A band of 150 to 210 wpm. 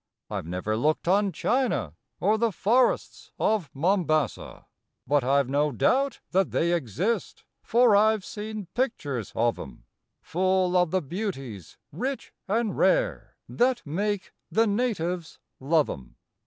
No: average, 140 wpm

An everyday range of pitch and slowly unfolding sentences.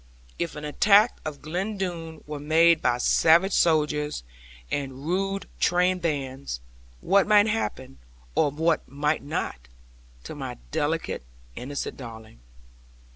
Yes: average, 4.1 semitones; slow, 125 wpm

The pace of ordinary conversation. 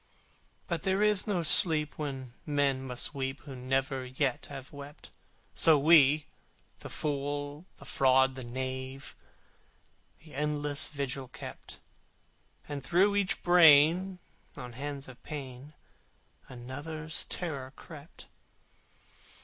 No: slow, 115 wpm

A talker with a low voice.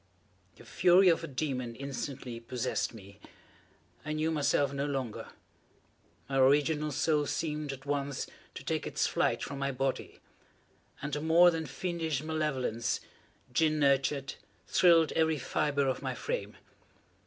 No: medium, 145 Hz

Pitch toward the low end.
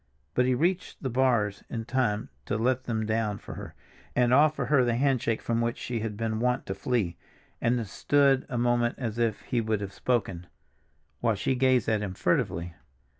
Yes: low, 120 Hz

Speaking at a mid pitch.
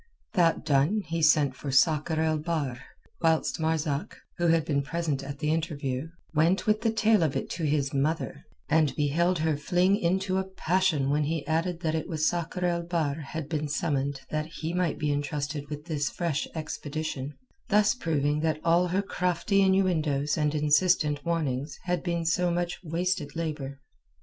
Yes: medium, 160 Hz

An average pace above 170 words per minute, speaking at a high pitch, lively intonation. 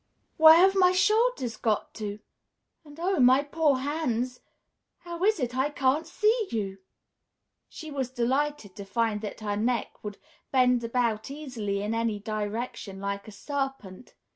No: average, 150 wpm; very high, 250 Hz; wide, 5.7 semitones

